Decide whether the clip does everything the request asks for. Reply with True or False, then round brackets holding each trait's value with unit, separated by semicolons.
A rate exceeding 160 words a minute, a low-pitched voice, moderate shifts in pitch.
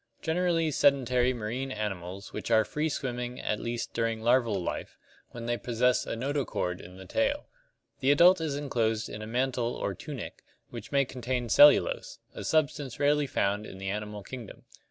True (170 wpm; 125 Hz; 4.5 semitones)